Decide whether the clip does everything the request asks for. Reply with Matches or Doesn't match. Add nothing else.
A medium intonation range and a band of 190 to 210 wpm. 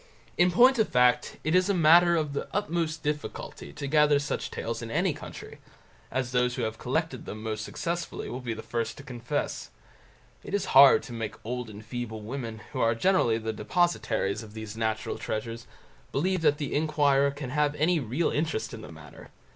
Doesn't match